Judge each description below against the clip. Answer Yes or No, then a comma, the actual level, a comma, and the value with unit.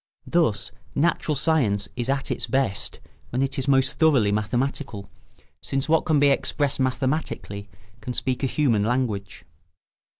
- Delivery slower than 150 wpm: Yes, average, 140 wpm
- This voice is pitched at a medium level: No, low, 130 Hz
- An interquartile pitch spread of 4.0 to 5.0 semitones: Yes, average, 4.6 semitones